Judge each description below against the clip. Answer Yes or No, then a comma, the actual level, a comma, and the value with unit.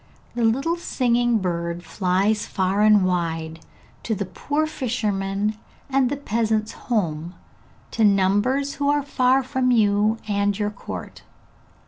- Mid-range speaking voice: No, high, 215 Hz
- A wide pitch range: No, average, 4.5 semitones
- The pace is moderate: No, slow, 130 wpm